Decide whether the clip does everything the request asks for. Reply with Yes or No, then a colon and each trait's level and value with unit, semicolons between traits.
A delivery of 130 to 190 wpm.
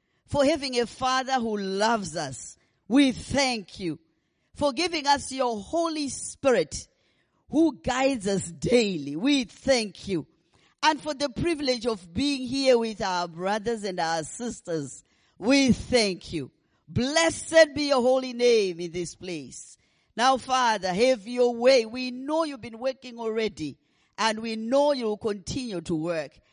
Yes: average, 145 wpm